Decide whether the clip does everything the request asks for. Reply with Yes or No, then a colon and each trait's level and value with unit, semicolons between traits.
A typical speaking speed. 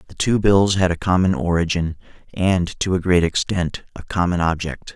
Yes: average, 180 wpm